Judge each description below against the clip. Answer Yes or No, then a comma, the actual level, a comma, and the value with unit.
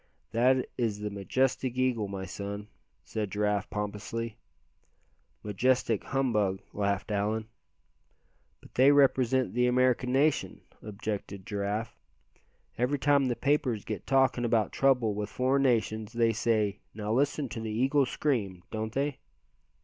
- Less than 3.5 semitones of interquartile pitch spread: No, average, 3.8 semitones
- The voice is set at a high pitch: No, low, 115 Hz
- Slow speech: Yes, slow, 130 wpm